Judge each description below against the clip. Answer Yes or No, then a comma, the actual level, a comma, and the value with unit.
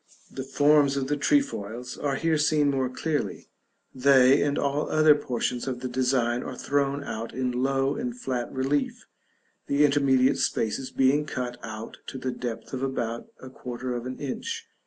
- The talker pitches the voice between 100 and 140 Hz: Yes, low, 135 Hz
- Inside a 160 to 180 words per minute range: Yes, average, 175 wpm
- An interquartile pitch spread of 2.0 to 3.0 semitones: Yes, narrow, 2.4 semitones